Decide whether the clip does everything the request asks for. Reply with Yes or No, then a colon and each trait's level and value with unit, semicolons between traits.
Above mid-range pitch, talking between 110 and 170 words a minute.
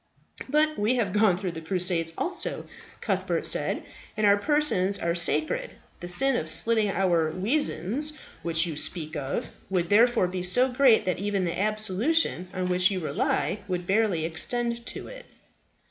Yes: high, 195 Hz; average, 160 wpm